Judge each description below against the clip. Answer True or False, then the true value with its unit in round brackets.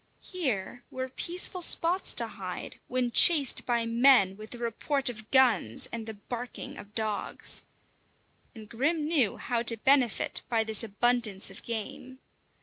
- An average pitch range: True (3.2 semitones)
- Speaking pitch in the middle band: False (240 Hz)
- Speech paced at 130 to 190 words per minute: True (145 wpm)